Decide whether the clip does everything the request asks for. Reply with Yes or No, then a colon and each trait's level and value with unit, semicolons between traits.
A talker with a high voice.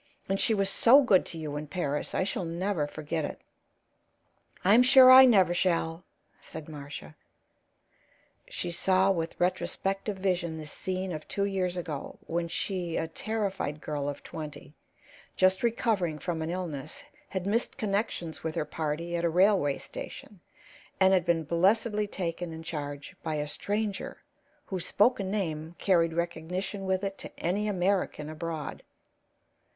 No: medium, 175 Hz